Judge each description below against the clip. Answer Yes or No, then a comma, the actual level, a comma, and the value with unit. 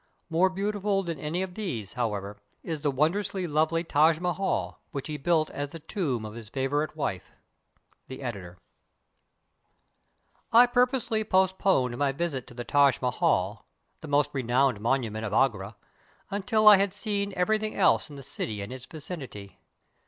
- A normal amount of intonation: No, wide, 7.4 semitones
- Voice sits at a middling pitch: Yes, medium, 150 Hz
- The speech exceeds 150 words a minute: Yes, average, 165 wpm